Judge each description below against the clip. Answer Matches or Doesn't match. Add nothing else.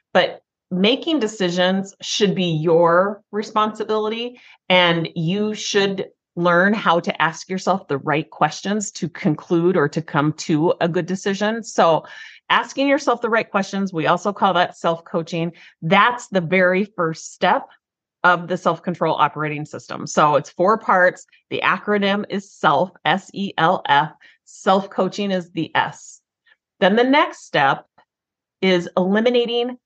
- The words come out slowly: Doesn't match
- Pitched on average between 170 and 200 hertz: Matches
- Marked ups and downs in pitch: Doesn't match